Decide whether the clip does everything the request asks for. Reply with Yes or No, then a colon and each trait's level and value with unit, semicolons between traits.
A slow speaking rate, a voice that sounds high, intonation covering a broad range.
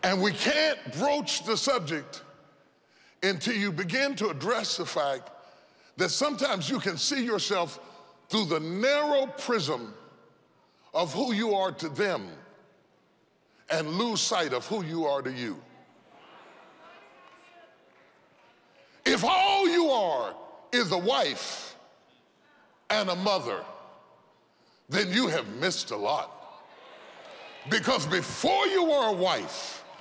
Yes: slow, 120 wpm; high, 215 Hz; wide, 7.2 semitones